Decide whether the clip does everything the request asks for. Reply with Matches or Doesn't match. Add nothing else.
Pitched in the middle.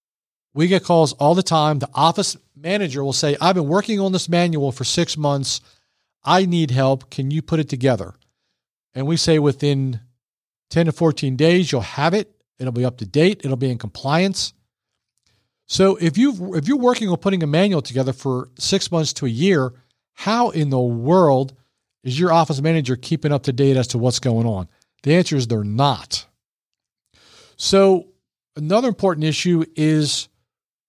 Matches